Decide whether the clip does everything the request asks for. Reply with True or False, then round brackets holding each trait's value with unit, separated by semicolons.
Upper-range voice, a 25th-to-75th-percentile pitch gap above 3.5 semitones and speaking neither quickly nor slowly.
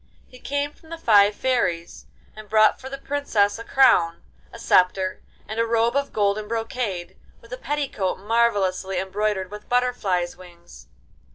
True (215 Hz; 4.7 semitones; 155 wpm)